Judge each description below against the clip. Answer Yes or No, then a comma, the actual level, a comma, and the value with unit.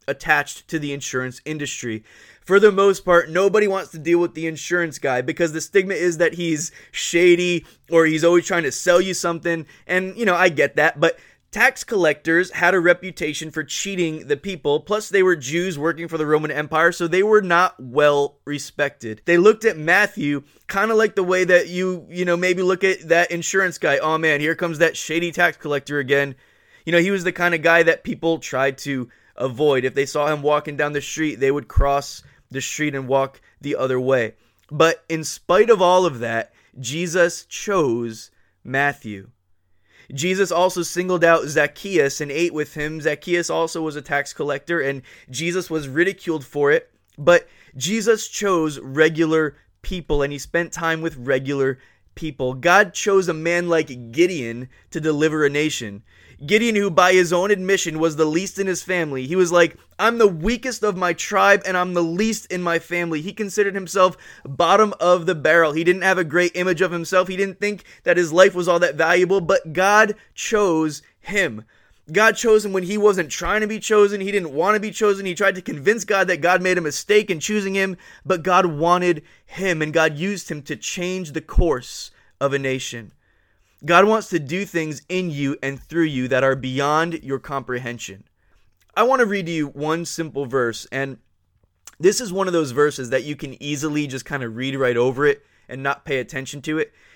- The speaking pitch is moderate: Yes, medium, 165 Hz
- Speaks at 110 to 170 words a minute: No, average, 200 wpm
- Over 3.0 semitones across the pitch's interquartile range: Yes, average, 4.4 semitones